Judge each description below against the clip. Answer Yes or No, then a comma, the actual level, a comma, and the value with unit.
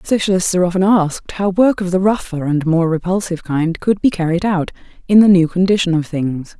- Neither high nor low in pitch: Yes, medium, 180 Hz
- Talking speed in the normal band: No, fast, 210 wpm